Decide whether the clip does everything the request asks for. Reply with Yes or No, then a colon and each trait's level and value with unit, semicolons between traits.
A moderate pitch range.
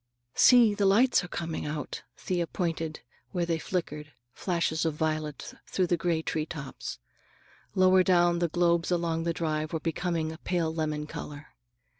No: narrow, 2.1 semitones